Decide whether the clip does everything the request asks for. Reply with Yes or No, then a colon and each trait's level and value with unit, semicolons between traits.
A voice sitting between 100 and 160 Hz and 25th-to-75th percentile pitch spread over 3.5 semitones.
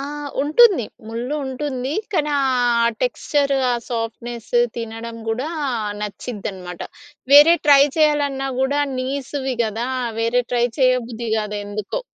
No: very high, 255 Hz; average, 4.0 semitones